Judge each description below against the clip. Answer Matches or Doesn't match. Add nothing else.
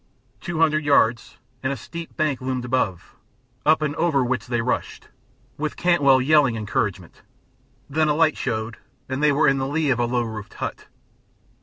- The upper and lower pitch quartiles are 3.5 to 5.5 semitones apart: Matches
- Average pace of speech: Matches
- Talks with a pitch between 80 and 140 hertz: Matches